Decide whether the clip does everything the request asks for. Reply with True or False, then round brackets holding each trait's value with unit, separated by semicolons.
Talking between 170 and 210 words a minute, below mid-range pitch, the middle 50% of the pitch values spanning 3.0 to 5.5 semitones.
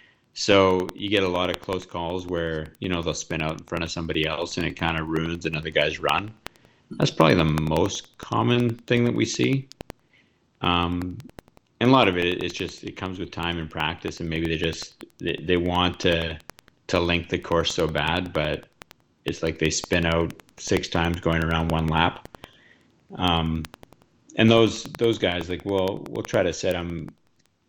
False (190 wpm; 85 Hz; 2.4 semitones)